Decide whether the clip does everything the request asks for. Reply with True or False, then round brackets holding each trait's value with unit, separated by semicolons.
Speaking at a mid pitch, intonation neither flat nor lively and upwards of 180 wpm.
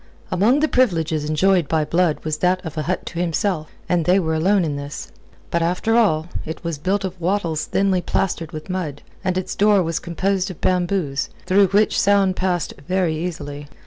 True (180 Hz; 3.3 semitones; 190 wpm)